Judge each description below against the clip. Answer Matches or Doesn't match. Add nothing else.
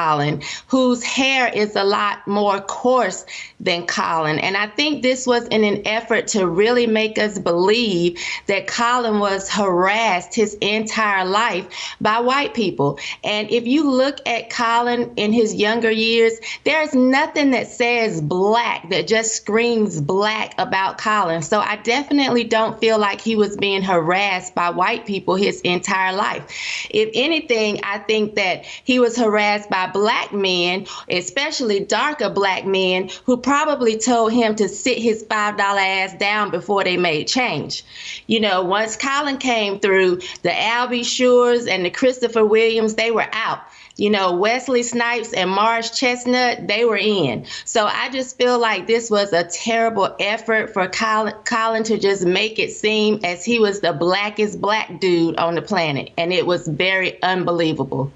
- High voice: Matches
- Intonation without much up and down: Doesn't match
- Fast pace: Doesn't match